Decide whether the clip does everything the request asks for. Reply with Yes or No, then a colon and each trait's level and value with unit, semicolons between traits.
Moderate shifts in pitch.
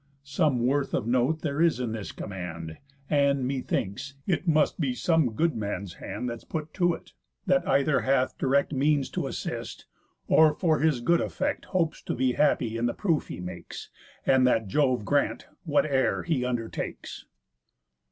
Yes: average, 4.3 semitones